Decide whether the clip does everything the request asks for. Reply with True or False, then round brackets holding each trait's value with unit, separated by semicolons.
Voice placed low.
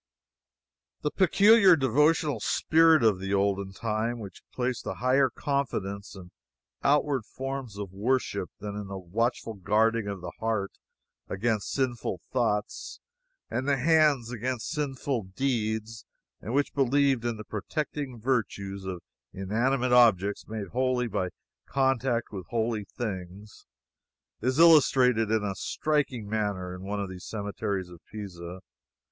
True (115 Hz)